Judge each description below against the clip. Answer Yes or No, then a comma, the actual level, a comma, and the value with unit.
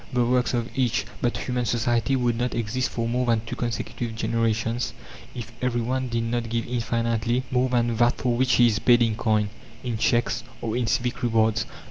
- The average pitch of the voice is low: Yes, low, 120 Hz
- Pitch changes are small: Yes, narrow, 1.3 semitones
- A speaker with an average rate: Yes, average, 190 wpm